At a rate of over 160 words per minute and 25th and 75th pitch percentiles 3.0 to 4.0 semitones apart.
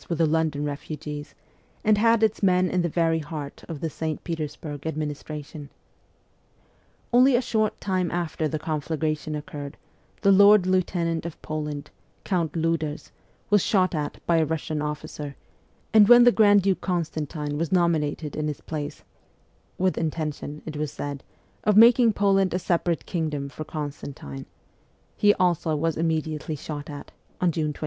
No: average, 155 wpm; average, 3.4 semitones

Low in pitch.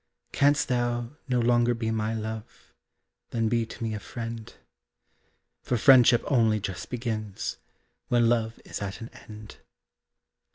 Yes: low, 115 Hz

